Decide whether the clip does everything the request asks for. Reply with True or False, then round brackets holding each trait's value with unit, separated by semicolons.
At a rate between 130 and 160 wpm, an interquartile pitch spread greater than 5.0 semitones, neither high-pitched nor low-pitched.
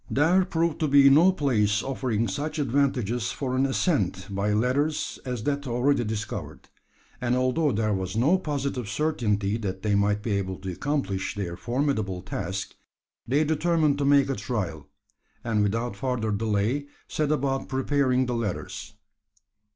False (150 wpm; 5.4 semitones; 125 Hz)